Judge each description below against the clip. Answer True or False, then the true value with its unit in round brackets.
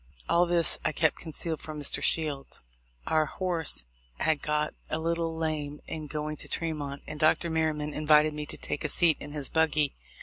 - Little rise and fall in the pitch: True (1.3 semitones)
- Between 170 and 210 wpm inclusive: True (180 wpm)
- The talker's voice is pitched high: False (155 Hz)